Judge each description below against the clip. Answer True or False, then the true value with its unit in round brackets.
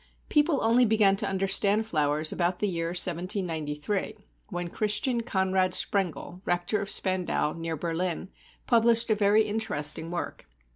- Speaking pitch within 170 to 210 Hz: True (190 Hz)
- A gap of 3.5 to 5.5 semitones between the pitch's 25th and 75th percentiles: True (3.9 semitones)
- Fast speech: False (135 wpm)